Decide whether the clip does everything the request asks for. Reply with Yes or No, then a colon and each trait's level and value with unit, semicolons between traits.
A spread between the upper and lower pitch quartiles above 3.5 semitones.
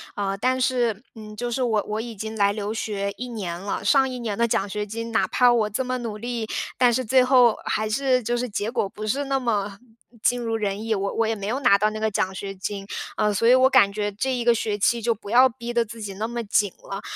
No: average, 2.7 semitones